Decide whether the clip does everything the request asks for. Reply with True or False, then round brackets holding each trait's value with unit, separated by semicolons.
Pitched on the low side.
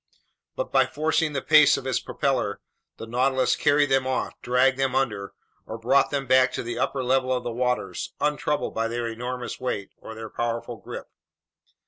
True (130 Hz)